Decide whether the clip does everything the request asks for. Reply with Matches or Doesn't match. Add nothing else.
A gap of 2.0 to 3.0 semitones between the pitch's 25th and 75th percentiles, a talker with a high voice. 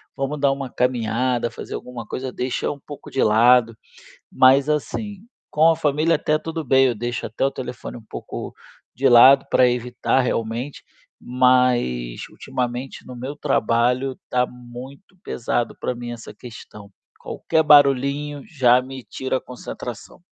Doesn't match